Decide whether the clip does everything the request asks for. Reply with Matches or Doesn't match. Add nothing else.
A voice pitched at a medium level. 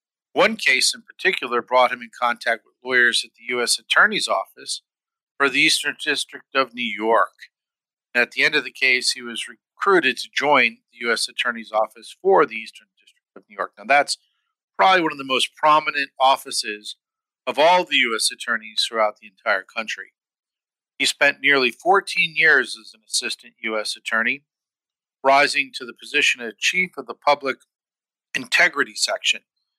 Doesn't match